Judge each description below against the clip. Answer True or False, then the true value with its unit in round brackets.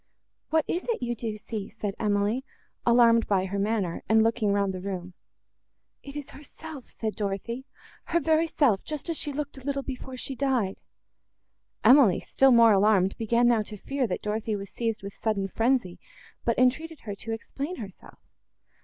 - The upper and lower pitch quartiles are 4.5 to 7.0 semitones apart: True (4.9 semitones)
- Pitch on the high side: True (230 Hz)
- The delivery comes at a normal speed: True (175 wpm)